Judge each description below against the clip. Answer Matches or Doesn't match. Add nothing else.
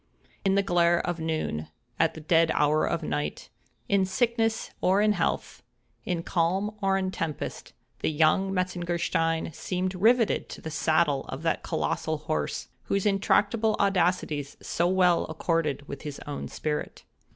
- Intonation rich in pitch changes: Doesn't match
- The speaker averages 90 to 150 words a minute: Matches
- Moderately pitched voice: Matches